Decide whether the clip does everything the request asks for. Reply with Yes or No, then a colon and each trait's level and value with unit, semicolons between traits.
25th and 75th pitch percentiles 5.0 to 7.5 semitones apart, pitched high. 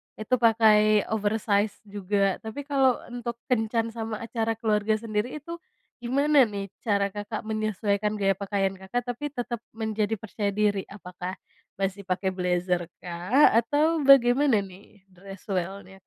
No: average, 3.0 semitones; high, 215 Hz